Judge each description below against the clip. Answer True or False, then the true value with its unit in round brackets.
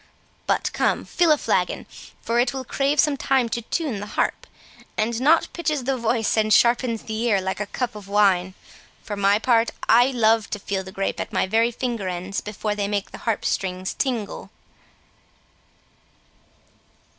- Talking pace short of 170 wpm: False (175 wpm)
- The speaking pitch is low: False (225 Hz)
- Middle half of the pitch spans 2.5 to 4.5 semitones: True (3.6 semitones)